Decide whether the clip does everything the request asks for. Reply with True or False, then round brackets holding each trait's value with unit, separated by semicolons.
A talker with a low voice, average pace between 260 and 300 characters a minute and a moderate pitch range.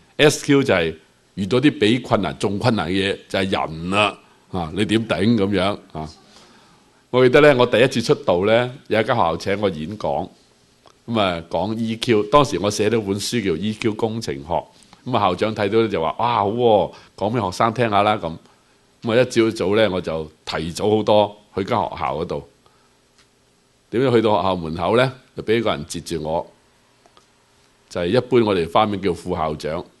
True (105 Hz; 280 characters per minute; 4.2 semitones)